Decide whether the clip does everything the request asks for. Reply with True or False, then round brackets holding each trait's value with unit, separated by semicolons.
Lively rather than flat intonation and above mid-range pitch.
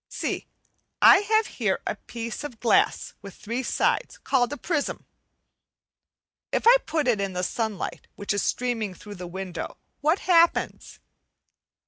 True (7.1 semitones; 235 Hz)